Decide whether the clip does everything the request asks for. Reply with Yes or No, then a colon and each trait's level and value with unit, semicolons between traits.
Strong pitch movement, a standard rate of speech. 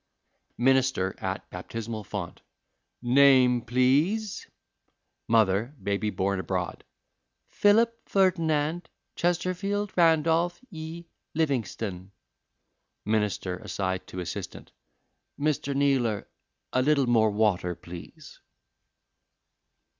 No: wide, 7.8 semitones; slow, 80 wpm